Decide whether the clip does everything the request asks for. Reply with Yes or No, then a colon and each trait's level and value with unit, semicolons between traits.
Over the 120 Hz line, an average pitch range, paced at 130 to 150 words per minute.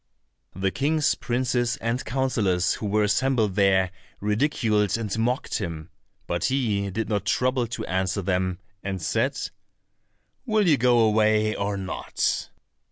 No: low, 105 Hz; average, 4.3 semitones; slow, 135 wpm